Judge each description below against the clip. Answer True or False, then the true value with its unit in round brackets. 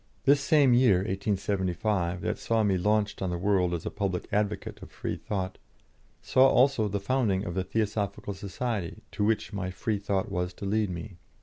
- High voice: False (100 Hz)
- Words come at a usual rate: True (175 wpm)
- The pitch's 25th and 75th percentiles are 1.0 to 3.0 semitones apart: True (2.7 semitones)